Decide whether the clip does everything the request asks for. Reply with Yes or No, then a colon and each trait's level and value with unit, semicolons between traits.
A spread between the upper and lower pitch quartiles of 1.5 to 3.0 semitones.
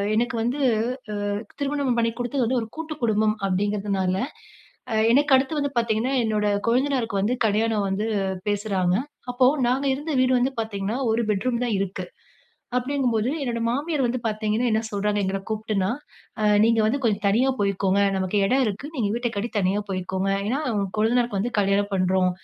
No: average, 3.7 semitones